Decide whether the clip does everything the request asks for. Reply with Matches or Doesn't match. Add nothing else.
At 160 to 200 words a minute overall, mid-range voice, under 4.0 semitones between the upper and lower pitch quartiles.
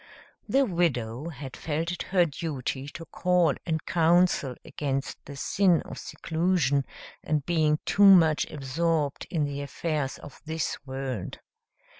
Doesn't match